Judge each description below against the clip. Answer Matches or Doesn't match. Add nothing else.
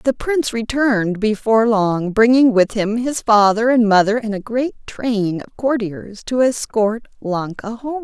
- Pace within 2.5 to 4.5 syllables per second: Matches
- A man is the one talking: Doesn't match